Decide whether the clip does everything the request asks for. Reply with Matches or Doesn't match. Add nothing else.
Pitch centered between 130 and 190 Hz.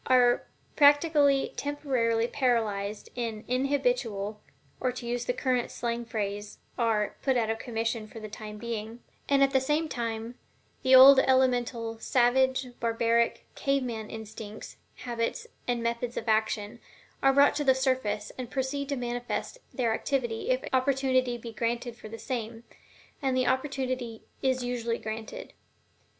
Doesn't match